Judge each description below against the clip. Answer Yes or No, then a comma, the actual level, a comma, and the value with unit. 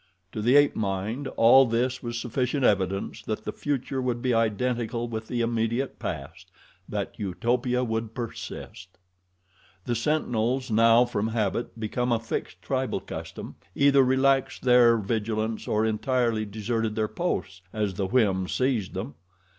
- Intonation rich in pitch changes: No, average, 2.7 semitones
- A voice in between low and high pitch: No, low, 115 Hz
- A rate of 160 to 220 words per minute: No, average, 145 wpm